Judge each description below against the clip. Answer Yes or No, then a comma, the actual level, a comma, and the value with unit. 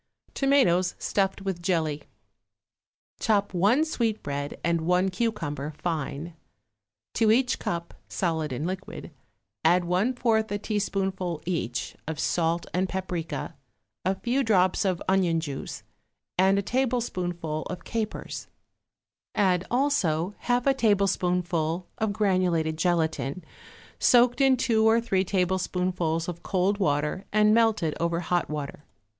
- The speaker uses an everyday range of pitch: Yes, average, 4.2 semitones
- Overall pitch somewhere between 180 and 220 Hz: Yes, medium, 185 Hz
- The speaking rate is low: Yes, slow, 125 wpm